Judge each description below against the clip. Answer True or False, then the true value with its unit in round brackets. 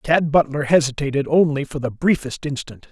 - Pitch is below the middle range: False (145 Hz)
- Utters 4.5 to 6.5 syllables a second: True (5.2 syllables/s)